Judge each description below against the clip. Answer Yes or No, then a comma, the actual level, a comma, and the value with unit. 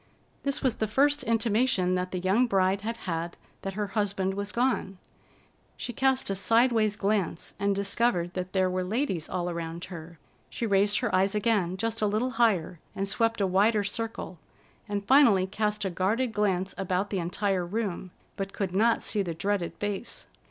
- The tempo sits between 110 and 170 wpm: No, average, 180 wpm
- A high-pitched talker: Yes, high, 200 Hz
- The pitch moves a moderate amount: Yes, average, 3.4 semitones